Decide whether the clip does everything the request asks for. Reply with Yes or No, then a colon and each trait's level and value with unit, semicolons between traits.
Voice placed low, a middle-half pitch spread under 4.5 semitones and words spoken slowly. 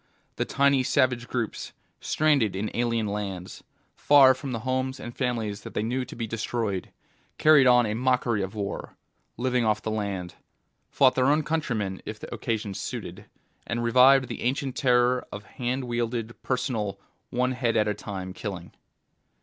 No: low, 120 Hz; average, 3.5 semitones; average, 165 wpm